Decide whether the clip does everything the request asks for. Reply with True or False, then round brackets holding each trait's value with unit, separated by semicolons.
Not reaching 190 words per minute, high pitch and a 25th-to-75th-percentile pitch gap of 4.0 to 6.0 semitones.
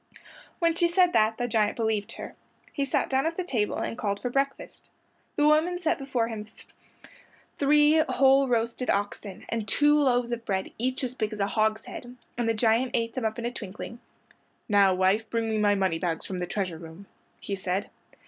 False (195 wpm; 230 Hz; 4.6 semitones)